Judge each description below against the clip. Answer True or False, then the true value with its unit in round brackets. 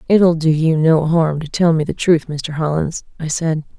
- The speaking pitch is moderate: True (160 Hz)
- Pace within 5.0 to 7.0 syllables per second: False (4.5 syllables/s)